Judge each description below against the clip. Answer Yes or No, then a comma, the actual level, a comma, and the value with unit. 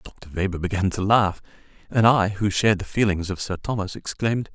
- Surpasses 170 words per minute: Yes, average, 200 wpm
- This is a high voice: No, low, 100 Hz